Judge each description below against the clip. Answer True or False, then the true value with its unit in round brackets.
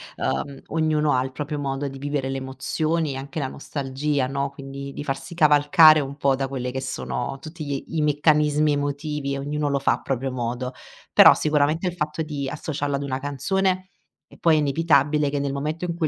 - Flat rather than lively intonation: True (1.9 semitones)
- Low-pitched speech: False (145 Hz)